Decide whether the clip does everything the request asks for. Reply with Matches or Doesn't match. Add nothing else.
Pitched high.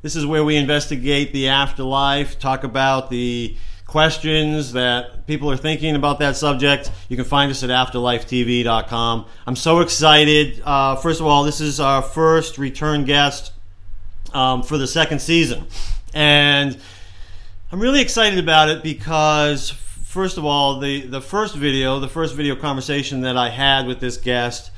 Doesn't match